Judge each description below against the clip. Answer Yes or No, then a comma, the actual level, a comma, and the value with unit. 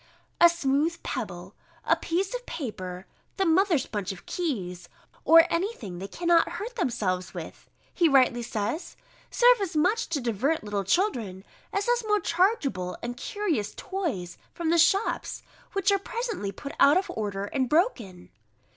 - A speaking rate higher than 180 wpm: No, average, 155 wpm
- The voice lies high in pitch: Yes, very high, 305 Hz